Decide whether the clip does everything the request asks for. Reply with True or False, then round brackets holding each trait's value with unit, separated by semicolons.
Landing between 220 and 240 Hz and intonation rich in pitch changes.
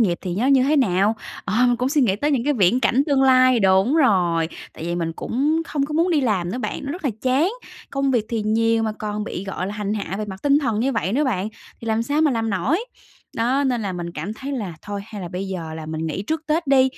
True (225 Hz; 6.0 semitones)